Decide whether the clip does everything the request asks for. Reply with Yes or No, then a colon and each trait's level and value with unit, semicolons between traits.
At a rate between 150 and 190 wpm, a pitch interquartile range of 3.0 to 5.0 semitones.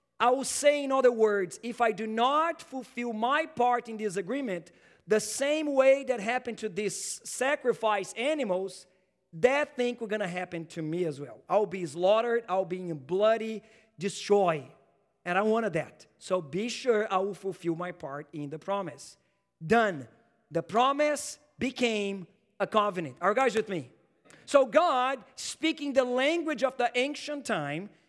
No: average, 170 wpm; wide, 5.6 semitones